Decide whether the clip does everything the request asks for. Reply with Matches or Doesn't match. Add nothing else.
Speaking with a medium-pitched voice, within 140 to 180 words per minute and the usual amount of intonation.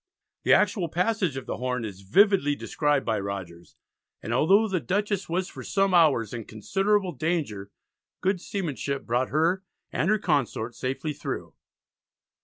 Doesn't match